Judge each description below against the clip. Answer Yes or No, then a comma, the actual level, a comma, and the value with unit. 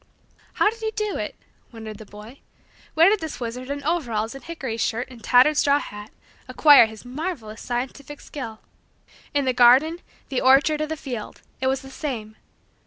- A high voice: Yes, very high, 260 Hz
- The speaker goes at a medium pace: Yes, average, 175 wpm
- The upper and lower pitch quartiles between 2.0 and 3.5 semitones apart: No, average, 4.8 semitones